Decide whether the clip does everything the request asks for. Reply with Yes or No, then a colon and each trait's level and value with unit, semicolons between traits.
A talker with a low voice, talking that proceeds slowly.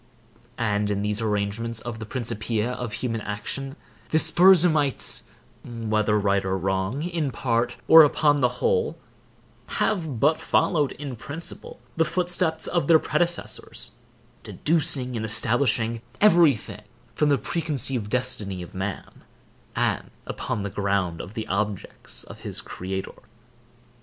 Yes: low, 120 Hz; slow, 130 wpm